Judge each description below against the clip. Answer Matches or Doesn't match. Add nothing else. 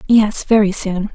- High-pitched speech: Matches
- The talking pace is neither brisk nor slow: Matches